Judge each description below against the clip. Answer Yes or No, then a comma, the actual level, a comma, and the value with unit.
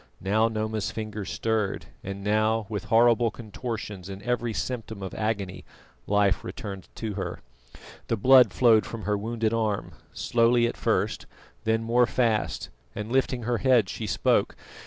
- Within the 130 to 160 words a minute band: Yes, average, 150 wpm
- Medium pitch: No, low, 110 Hz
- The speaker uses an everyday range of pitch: No, narrow, 2.2 semitones